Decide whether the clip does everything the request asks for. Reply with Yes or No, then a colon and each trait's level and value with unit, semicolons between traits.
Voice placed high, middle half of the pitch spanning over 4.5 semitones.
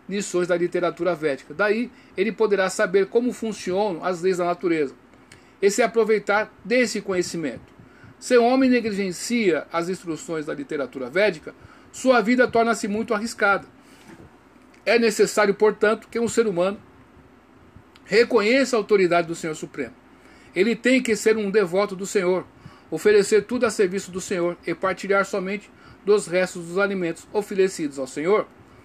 No: high, 205 Hz; average, 3.5 semitones